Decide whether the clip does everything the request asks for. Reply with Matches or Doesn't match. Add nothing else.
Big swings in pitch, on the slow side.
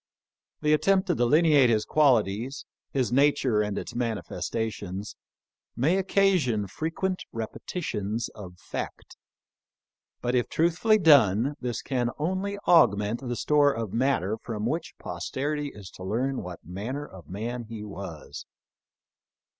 Matches